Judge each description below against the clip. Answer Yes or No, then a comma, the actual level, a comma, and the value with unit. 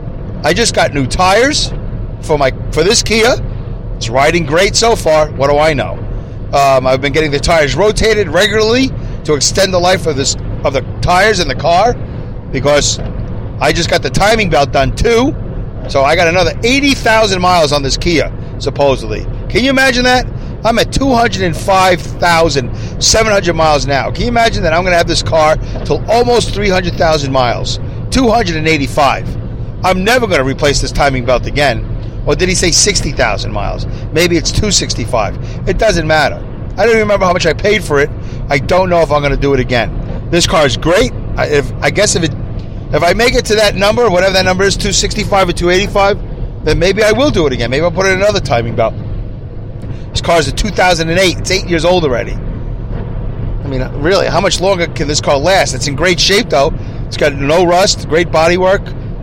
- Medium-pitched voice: Yes, medium, 145 Hz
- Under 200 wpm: No, fast, 205 wpm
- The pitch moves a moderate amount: No, wide, 7.5 semitones